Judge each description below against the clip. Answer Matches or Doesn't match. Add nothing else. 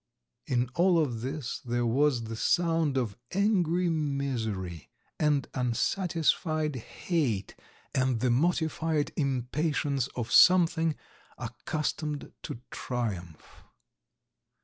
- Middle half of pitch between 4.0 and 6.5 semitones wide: Matches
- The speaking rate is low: Matches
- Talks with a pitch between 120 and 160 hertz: Matches